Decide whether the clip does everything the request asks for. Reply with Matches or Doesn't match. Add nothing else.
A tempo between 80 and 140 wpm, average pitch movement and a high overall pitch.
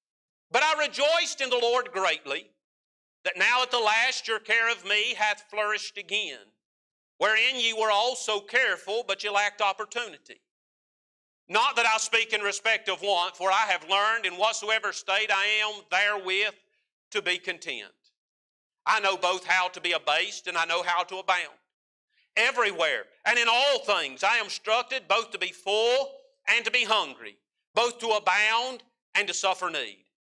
Doesn't match